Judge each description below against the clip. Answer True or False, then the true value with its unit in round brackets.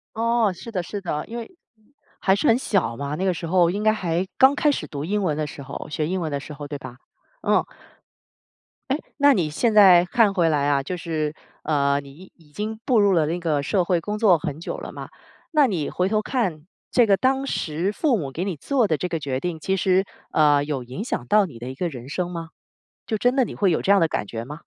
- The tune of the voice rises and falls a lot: True (5.8 semitones)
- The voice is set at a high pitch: False (175 Hz)